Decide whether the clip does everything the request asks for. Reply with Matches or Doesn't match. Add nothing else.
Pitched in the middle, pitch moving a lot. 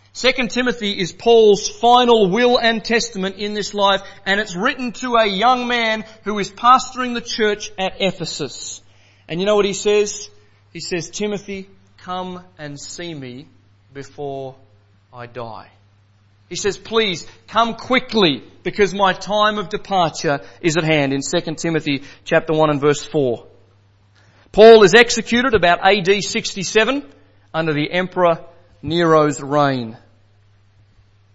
Matches